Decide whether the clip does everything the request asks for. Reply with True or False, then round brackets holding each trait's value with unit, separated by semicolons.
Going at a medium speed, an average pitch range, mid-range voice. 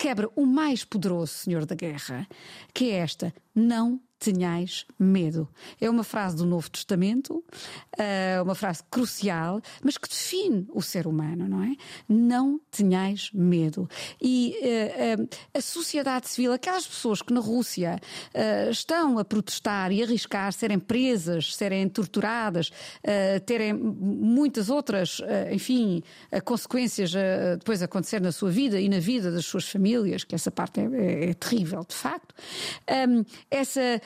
False (135 wpm; 5.0 semitones; 205 Hz)